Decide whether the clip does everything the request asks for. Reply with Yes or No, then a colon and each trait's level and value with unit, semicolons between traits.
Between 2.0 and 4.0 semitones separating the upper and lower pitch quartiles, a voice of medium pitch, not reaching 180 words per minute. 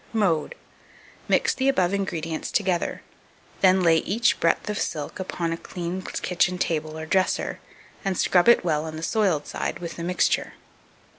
Yes: average, 2.9 semitones; medium, 180 Hz; average, 160 wpm